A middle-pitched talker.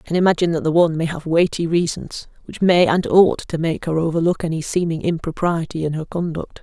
Yes: medium, 165 Hz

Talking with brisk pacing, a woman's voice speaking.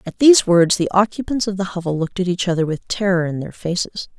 Yes: fast, 245 wpm; female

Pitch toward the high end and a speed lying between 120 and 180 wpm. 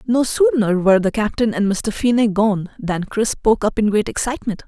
No: high, 215 Hz; fast, 205 wpm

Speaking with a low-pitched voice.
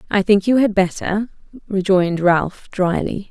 No: high, 195 Hz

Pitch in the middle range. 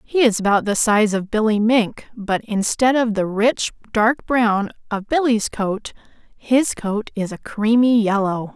No: high, 220 Hz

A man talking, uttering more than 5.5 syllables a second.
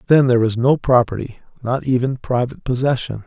Yes: male; 6.0 syllables/s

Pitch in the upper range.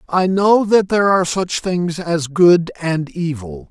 No: medium, 170 Hz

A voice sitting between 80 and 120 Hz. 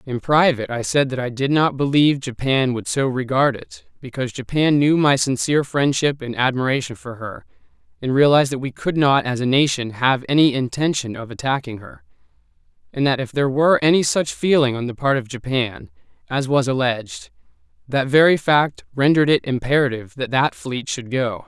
No: low, 135 Hz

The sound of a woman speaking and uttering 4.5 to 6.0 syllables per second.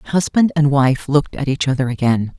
Yes: female; 5.2 syllables/s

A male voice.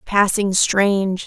No: female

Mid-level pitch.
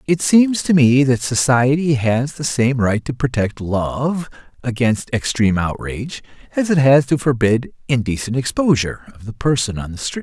No: low, 130 Hz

